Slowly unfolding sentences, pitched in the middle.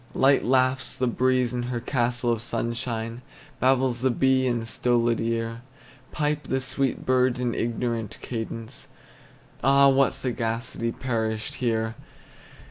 No: slow, 130 wpm; low, 120 Hz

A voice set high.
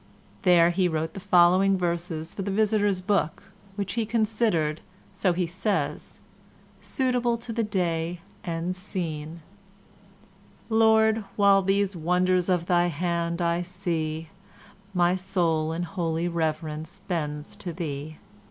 No: medium, 180 Hz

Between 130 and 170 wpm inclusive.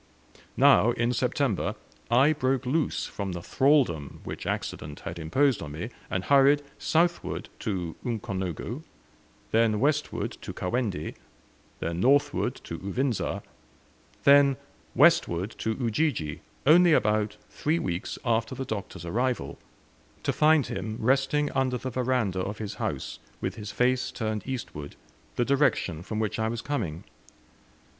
Yes: slow, 135 wpm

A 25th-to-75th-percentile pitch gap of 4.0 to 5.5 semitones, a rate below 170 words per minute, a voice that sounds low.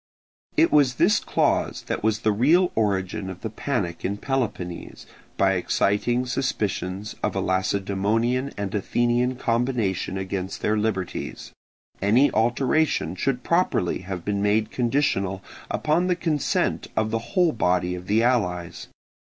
Yes: average, 4.8 semitones; slow, 135 wpm; low, 110 Hz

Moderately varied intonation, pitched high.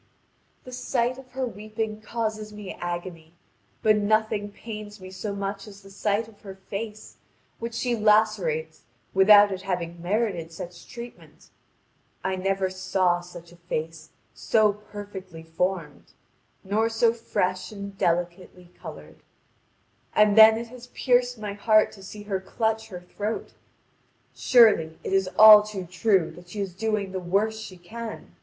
Yes: average, 3.1 semitones; high, 205 Hz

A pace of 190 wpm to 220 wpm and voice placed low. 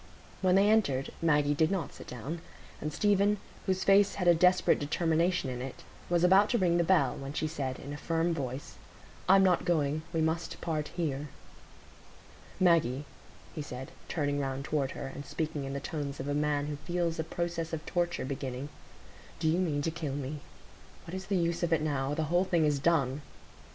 No: average, 195 wpm; medium, 160 Hz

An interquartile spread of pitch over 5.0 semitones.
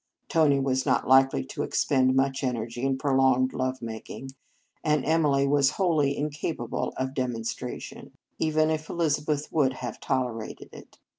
No: narrow, 2.6 semitones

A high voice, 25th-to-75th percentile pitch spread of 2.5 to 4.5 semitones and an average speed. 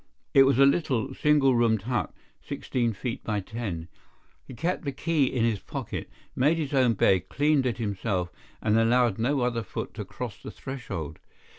No: low, 120 Hz; average, 3.8 semitones; average, 175 wpm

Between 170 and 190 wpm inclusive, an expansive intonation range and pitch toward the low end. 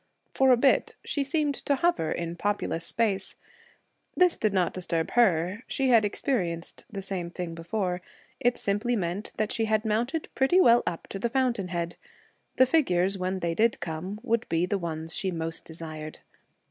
No: average, 175 wpm; wide, 5.7 semitones; high, 195 Hz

